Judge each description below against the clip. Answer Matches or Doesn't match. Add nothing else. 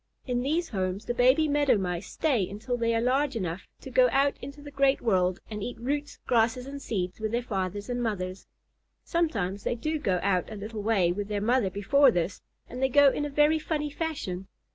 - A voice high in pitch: Matches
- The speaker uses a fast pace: Matches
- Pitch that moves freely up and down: Matches